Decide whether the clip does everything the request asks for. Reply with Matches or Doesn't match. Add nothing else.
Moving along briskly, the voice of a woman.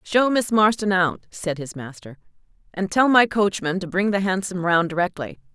Doesn't match